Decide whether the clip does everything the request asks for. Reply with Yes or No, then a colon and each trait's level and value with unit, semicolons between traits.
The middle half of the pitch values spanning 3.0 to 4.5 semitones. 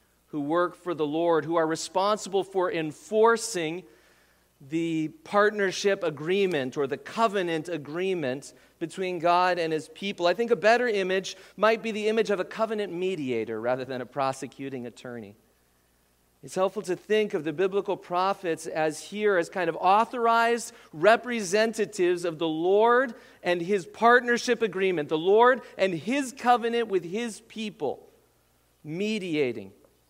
No: wide, 5.4 semitones